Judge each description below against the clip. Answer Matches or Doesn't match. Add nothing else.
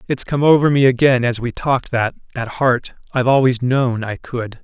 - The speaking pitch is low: Matches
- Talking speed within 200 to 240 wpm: Matches